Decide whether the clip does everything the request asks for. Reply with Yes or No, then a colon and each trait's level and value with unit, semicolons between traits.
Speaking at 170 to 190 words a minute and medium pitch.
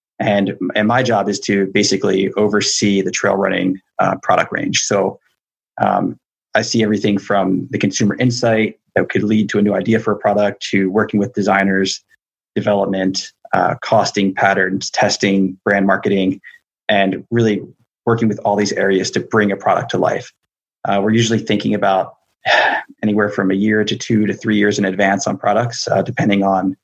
No: average, 175 wpm; low, 100 Hz